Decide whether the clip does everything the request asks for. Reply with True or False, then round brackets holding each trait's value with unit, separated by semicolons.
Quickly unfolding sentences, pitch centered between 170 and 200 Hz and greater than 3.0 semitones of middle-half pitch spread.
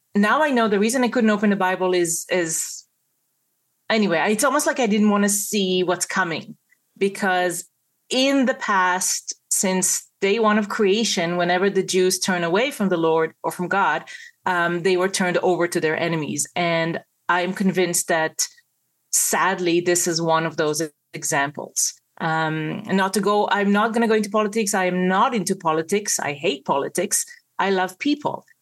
False (175 wpm; 185 Hz; 3.5 semitones)